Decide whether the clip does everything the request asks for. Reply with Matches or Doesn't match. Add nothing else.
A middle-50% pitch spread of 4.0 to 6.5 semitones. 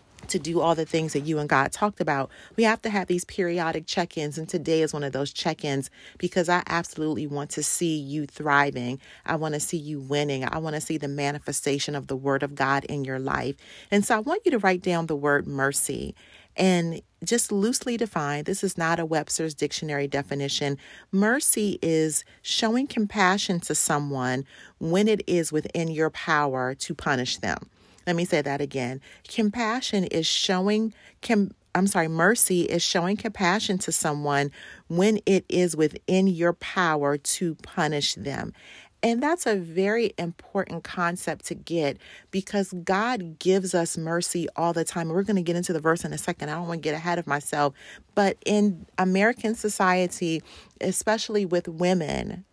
Matches